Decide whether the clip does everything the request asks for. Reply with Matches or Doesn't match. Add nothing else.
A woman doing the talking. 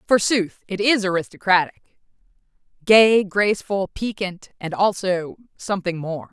Matches